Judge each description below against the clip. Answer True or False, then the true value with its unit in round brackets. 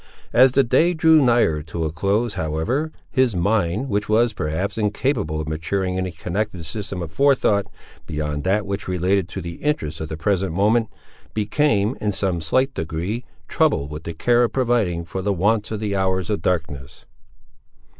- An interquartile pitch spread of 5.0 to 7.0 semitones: True (5.3 semitones)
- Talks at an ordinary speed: True (175 wpm)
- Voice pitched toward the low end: True (100 Hz)